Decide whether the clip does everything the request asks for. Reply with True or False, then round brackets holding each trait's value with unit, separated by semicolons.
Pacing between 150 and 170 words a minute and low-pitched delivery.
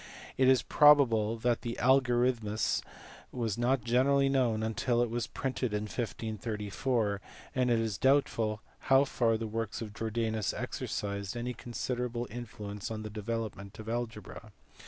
False (140 wpm; 115 Hz)